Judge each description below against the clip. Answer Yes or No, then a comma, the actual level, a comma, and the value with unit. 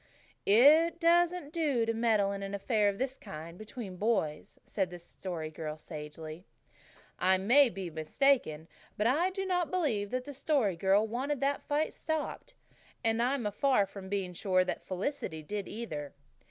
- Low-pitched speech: No, high, 210 Hz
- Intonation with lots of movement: Yes, wide, 7.2 semitones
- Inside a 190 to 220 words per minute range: No, average, 165 wpm